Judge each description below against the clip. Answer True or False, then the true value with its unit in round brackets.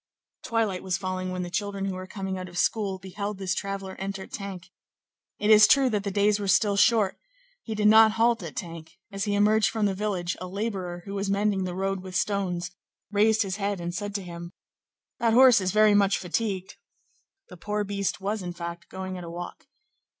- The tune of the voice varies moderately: False (2.2 semitones)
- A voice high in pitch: True (195 Hz)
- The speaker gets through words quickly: True (210 wpm)